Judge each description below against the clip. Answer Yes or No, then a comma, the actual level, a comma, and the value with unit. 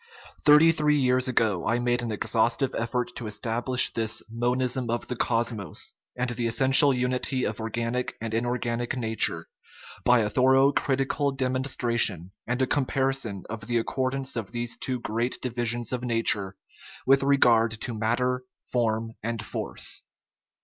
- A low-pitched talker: Yes, low, 120 Hz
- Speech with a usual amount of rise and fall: No, narrow, 2.2 semitones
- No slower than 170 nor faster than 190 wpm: No, average, 155 wpm